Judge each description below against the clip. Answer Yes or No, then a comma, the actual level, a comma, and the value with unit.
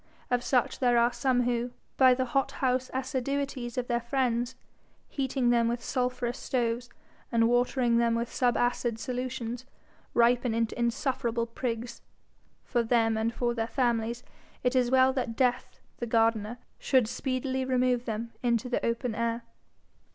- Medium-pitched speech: No, high, 245 Hz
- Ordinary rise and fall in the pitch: No, narrow, 1.5 semitones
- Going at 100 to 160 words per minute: Yes, average, 150 wpm